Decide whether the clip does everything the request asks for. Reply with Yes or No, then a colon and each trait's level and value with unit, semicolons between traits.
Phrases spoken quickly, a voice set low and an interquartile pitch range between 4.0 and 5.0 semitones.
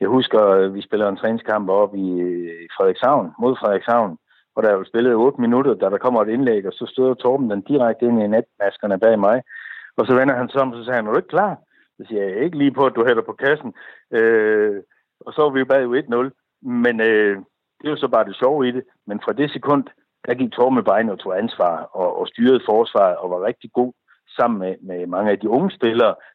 Yes: fast, 235 wpm; low, 120 Hz; average, 4.6 semitones